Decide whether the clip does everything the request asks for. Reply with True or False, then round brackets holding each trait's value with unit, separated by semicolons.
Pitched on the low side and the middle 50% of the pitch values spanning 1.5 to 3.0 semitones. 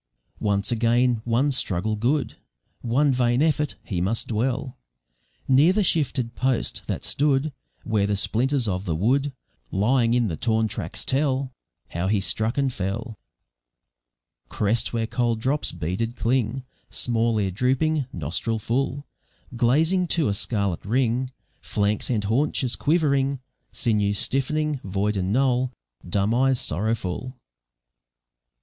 False (120 Hz; 4.2 semitones)